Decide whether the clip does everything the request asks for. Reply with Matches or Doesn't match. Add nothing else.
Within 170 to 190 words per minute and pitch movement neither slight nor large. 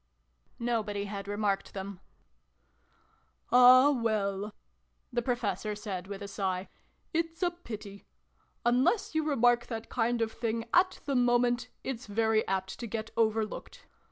Doesn't match